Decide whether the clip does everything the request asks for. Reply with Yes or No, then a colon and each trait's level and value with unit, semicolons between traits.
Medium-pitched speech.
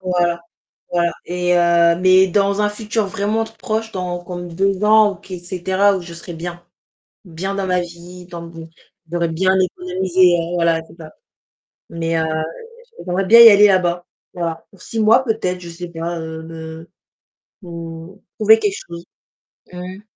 Yes: medium, 180 Hz